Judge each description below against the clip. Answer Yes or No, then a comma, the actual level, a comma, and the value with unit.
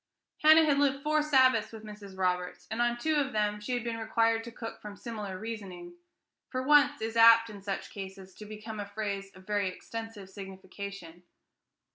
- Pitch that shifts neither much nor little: Yes, average, 3.3 semitones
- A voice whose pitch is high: Yes, high, 215 Hz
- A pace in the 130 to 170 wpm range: No, average, 185 wpm